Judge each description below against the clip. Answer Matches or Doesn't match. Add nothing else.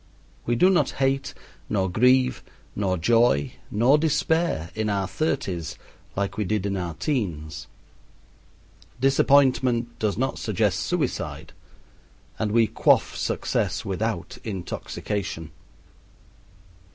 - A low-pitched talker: Matches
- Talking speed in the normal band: Doesn't match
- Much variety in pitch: Matches